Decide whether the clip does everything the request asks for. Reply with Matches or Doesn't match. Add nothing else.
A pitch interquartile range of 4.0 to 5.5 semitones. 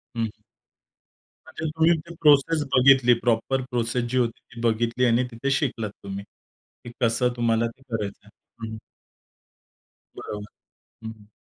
Doesn't match